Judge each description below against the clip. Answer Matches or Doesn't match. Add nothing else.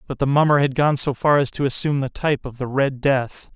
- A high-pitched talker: Doesn't match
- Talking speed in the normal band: Doesn't match